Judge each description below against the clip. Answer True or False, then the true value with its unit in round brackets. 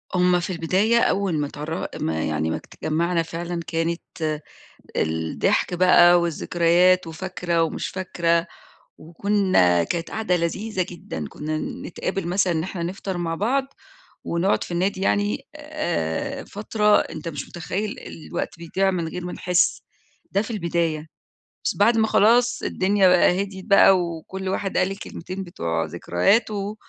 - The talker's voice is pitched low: False (180 Hz)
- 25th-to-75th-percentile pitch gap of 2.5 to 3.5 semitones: True (2.9 semitones)